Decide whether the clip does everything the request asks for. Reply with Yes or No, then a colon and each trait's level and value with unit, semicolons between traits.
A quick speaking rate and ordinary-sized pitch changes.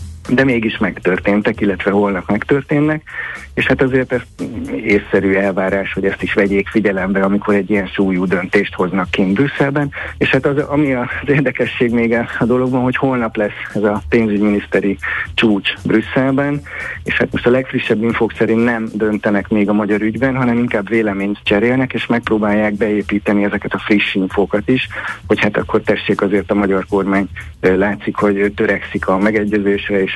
Yes: fast, 160 wpm; average, 3.4 semitones